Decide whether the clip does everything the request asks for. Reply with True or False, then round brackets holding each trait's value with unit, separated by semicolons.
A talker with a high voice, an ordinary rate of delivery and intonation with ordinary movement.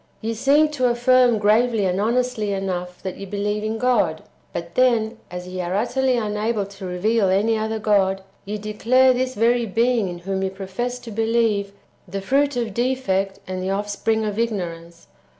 True (215 Hz; 175 wpm; 3.7 semitones)